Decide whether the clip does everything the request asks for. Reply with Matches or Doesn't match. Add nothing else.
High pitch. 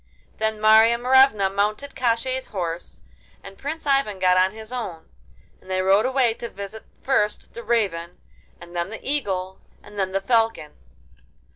Matches